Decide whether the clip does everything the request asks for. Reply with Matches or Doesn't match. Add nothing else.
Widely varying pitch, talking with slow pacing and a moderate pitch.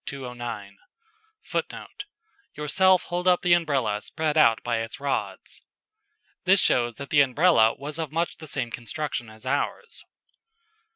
Matches